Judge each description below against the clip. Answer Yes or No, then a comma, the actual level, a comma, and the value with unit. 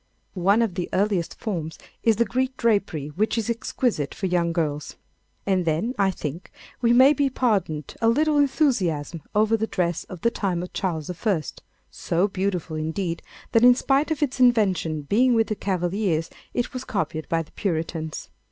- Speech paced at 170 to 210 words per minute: Yes, average, 175 wpm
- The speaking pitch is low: No, high, 195 Hz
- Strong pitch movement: Yes, wide, 5.9 semitones